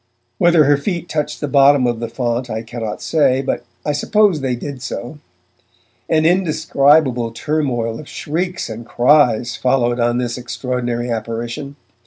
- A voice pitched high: No, low, 130 Hz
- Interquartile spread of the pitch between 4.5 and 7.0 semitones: No, average, 4.0 semitones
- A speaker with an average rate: Yes, average, 150 wpm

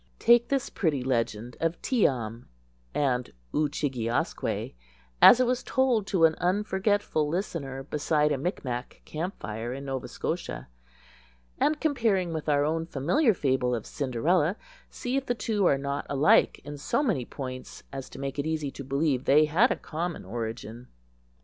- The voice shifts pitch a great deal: Yes, wide, 6.4 semitones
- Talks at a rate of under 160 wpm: No, average, 170 wpm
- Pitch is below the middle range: No, medium, 150 Hz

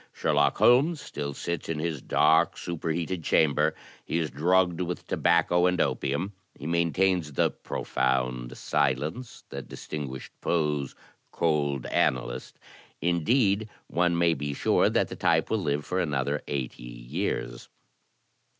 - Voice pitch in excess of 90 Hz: No, very low, 80 Hz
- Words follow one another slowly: Yes, slow, 130 wpm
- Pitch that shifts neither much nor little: Yes, average, 3.6 semitones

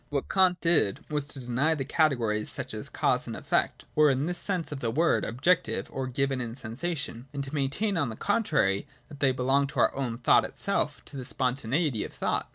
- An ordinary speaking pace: No, fast, 215 wpm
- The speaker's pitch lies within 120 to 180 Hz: Yes, medium, 140 Hz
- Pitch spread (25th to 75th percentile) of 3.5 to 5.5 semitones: Yes, average, 4.0 semitones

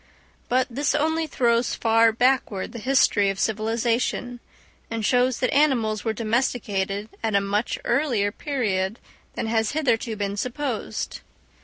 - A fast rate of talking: No, slow, 135 wpm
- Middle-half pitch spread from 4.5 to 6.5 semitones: No, average, 3.1 semitones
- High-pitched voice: Yes, high, 230 Hz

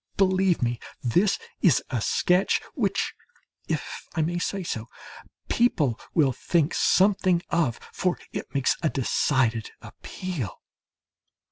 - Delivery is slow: Yes, slow, 120 wpm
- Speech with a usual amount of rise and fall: No, wide, 6.5 semitones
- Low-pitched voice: No, medium, 165 Hz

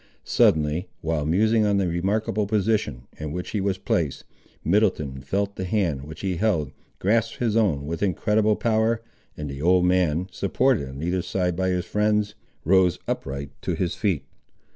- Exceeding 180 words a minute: No, average, 165 wpm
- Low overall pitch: Yes, very low, 95 Hz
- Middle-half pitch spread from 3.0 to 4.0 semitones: No, average, 4.8 semitones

